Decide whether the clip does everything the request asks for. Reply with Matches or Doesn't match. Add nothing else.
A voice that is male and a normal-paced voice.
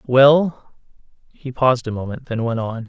Matches